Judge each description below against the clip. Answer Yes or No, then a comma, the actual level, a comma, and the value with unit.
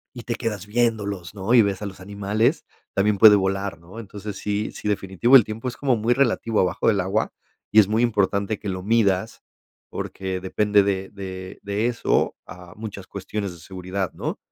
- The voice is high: No, low, 100 Hz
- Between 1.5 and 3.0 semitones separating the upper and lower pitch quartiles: Yes, narrow, 2.5 semitones